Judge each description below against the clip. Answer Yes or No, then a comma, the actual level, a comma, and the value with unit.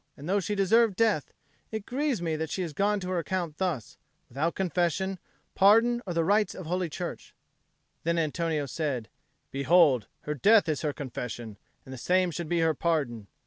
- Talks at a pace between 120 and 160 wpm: No, average, 185 wpm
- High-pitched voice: No, medium, 170 Hz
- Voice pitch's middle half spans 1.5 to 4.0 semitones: No, average, 4.4 semitones